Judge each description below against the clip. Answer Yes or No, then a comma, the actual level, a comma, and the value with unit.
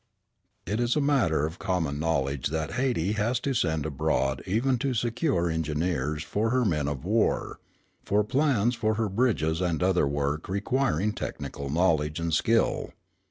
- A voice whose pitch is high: No, very low, 90 Hz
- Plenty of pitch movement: Yes, wide, 6.9 semitones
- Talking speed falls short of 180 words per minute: Yes, average, 160 wpm